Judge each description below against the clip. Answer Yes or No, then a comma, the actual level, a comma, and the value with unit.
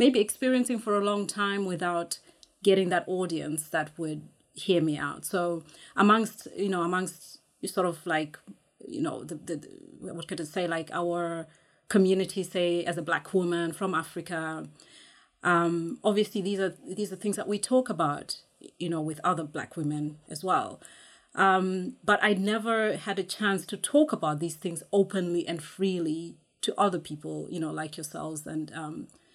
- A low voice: No, medium, 180 Hz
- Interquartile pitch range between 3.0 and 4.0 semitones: Yes, average, 3.5 semitones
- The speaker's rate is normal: Yes, average, 170 wpm